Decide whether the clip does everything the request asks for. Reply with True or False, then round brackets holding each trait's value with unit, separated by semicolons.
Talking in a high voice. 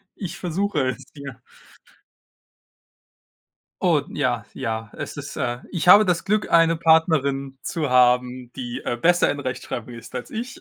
False (140 Hz)